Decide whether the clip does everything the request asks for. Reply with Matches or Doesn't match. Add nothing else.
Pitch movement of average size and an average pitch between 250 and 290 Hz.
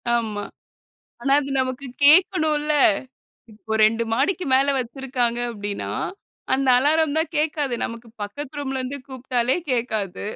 Matches